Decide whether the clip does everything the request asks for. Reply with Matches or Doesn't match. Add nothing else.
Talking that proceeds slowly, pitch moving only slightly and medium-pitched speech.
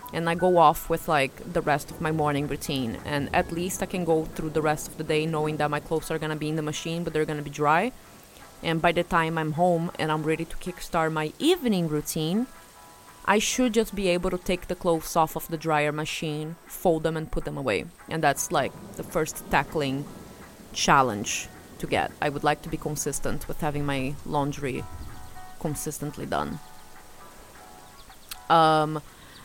Doesn't match